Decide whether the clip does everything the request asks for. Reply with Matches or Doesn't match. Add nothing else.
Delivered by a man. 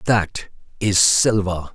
Matches